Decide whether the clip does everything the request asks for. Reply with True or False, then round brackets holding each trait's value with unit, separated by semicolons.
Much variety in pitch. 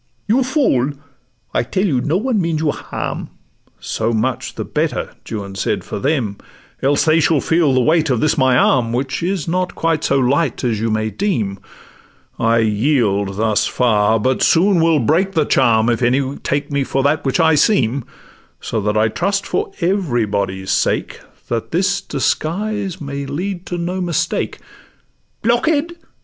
True (7.1 semitones)